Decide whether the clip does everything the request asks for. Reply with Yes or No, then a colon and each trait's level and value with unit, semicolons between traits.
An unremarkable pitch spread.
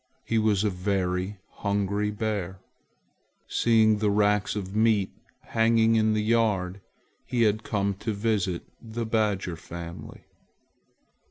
No: narrow, 2.2 semitones